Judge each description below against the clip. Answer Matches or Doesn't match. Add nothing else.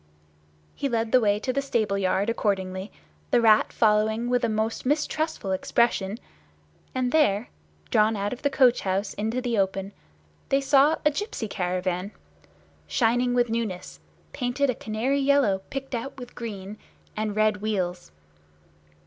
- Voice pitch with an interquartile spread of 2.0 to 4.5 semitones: Matches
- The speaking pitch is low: Doesn't match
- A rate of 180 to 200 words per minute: Doesn't match